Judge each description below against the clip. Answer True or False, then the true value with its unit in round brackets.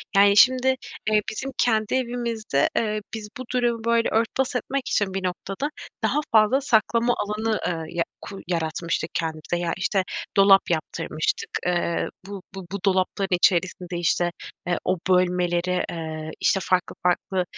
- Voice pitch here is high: True (195 Hz)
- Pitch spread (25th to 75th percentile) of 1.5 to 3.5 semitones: False (4.2 semitones)